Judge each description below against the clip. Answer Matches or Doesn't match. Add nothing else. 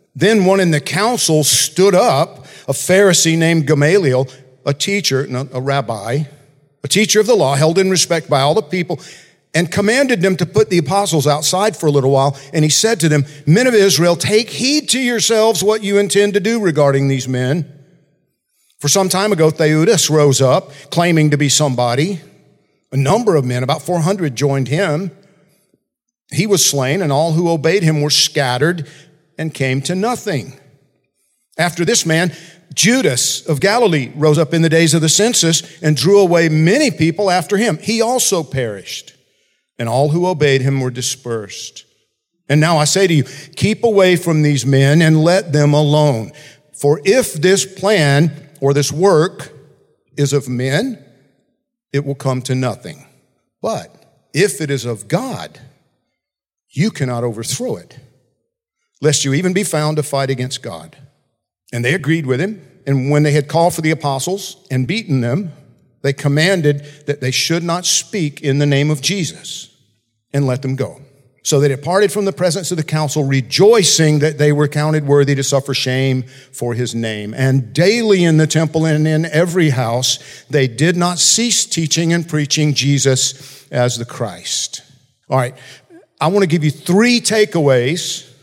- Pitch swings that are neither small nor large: Matches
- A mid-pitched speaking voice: Matches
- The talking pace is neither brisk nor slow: Matches